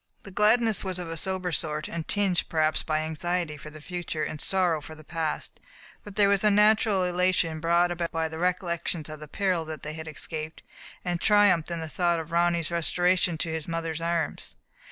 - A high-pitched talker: No, medium, 170 Hz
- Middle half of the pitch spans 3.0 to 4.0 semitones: No, narrow, 2.5 semitones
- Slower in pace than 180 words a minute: No, average, 200 wpm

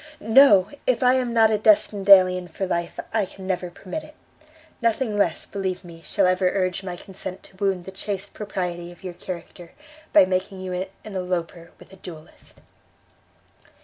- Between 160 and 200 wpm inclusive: Yes, average, 175 wpm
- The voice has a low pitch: No, high, 190 Hz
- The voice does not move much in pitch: Yes, narrow, 2.1 semitones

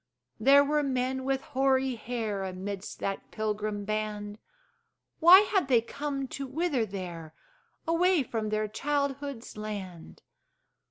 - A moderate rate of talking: No, slow, 120 wpm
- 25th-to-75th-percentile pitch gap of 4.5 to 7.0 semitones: Yes, average, 5.0 semitones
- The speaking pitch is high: Yes, high, 245 Hz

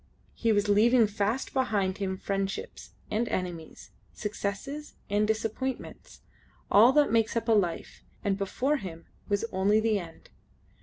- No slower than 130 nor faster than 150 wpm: Yes, average, 140 wpm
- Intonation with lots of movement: No, average, 2.7 semitones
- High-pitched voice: Yes, high, 210 Hz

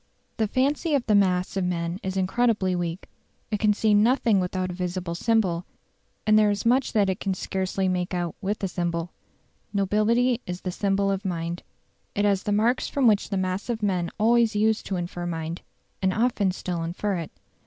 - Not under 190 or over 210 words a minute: Yes, average, 195 wpm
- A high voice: Yes, high, 195 Hz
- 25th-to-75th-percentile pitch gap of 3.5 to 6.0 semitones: No, average, 3.1 semitones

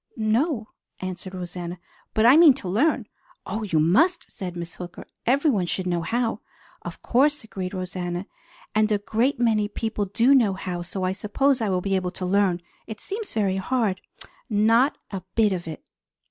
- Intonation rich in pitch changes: No, average, 4.4 semitones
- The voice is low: No, high, 205 Hz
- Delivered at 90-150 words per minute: No, average, 175 wpm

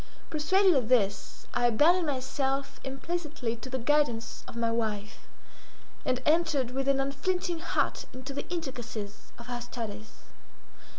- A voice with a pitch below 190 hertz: No, very high, 265 Hz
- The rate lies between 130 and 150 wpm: Yes, slow, 135 wpm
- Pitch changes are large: No, average, 4.4 semitones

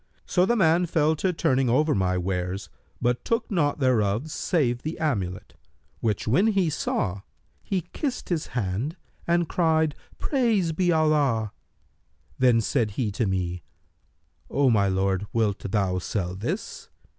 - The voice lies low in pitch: Yes, low, 130 Hz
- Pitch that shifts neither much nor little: No, wide, 8.8 semitones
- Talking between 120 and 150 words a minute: Yes, average, 145 wpm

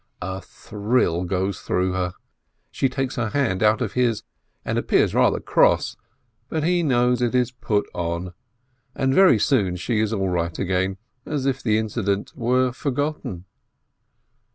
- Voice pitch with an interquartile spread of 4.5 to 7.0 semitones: Yes, wide, 5.4 semitones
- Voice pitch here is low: Yes, low, 110 Hz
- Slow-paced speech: No, average, 155 wpm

